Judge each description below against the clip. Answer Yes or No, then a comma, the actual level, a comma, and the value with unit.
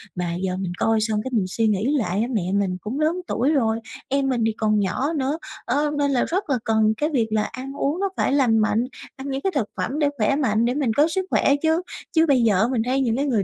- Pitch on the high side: Yes, very high, 250 Hz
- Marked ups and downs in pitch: No, average, 4.8 semitones